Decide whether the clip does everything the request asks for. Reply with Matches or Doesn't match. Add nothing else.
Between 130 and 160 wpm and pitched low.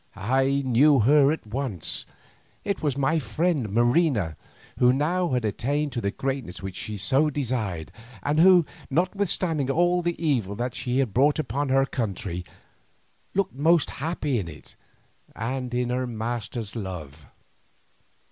Matches